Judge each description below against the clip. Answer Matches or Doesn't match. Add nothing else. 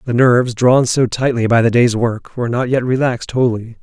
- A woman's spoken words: Doesn't match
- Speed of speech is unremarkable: Doesn't match